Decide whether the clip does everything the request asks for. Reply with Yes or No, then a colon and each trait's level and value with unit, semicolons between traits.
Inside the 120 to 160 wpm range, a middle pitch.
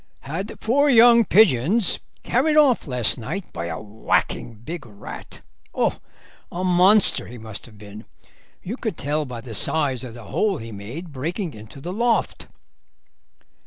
Yes: average, 155 wpm; medium, 150 Hz